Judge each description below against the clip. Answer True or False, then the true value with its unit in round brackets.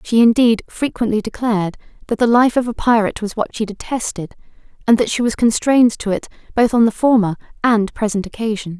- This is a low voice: False (220 Hz)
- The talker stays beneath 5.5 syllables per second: False (5.9 syllables/s)